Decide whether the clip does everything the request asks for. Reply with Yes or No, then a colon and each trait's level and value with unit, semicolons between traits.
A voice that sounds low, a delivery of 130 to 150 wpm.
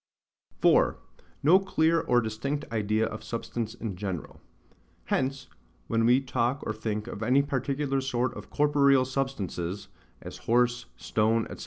Yes: low, 120 Hz; average, 140 wpm